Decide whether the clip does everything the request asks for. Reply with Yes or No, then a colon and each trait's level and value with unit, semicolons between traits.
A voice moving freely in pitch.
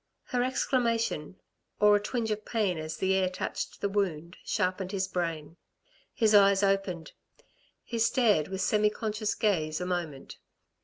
No: average, 3.2 semitones